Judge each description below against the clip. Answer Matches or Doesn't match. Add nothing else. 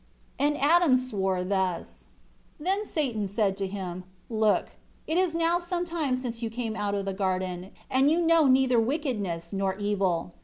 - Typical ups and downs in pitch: Doesn't match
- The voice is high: Matches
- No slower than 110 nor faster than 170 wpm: Doesn't match